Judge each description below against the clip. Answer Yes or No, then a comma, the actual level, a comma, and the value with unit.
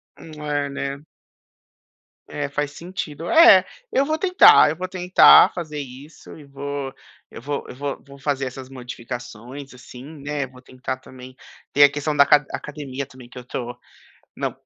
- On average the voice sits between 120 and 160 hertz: Yes, medium, 140 Hz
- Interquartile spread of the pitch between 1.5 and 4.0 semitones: Yes, narrow, 2.4 semitones